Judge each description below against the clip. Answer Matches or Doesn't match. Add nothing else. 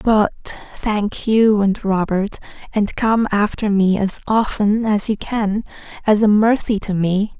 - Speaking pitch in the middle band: Doesn't match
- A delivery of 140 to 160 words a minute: Matches